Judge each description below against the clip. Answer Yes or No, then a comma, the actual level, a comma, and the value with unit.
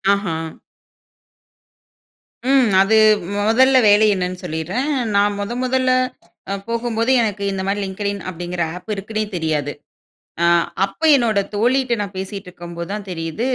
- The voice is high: Yes, high, 200 Hz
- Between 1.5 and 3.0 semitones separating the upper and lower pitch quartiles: No, average, 4.1 semitones